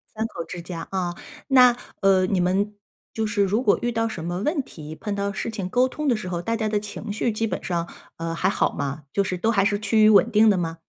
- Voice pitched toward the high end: Yes, high, 205 Hz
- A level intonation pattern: No, average, 3.7 semitones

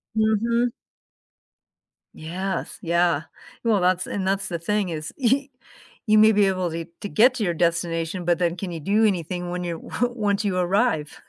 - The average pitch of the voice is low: No, medium, 185 Hz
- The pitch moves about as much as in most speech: Yes, average, 3.8 semitones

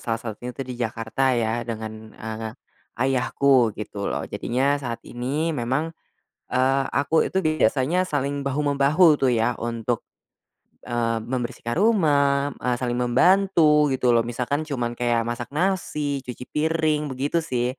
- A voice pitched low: Yes, low, 130 Hz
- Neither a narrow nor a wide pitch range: Yes, average, 3.9 semitones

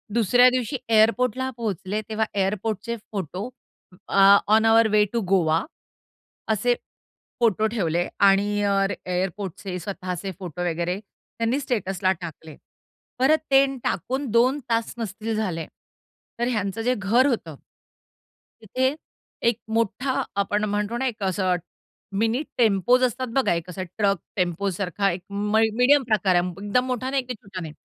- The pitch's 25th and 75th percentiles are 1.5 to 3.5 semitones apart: No, average, 3.9 semitones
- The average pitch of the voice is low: No, high, 210 Hz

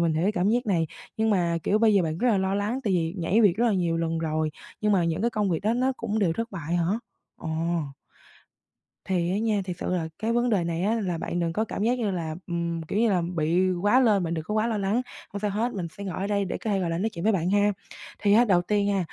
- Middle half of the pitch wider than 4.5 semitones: No, average, 4.0 semitones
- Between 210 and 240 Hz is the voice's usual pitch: No, high, 195 Hz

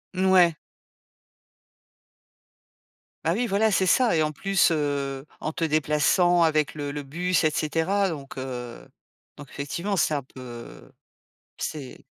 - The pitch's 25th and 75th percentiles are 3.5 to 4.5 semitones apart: Yes, average, 4.1 semitones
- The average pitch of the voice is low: No, medium, 155 Hz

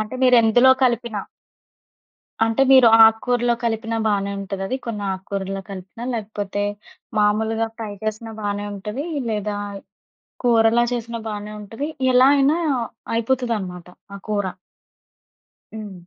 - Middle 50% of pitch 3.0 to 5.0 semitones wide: No, narrow, 2.5 semitones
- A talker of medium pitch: No, high, 220 Hz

